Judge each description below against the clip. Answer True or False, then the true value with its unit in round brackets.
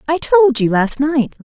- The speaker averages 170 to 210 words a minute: True (205 wpm)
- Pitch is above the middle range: True (270 Hz)